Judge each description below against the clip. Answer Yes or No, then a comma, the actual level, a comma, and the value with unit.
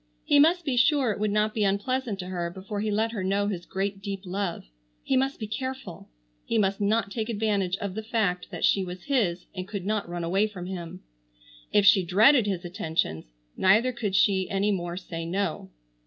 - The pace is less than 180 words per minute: No, fast, 205 wpm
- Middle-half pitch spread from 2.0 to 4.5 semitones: Yes, average, 3.1 semitones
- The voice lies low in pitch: No, high, 200 Hz